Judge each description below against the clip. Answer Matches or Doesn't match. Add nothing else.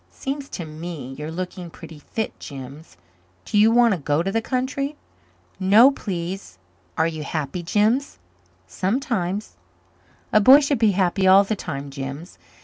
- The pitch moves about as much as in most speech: Doesn't match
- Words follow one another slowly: Doesn't match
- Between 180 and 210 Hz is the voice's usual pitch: Matches